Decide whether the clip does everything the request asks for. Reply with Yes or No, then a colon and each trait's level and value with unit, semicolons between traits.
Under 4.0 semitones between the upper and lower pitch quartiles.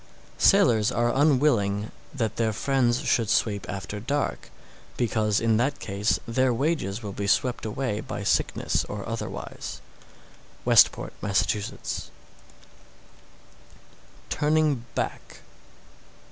No: average, 4.3 semitones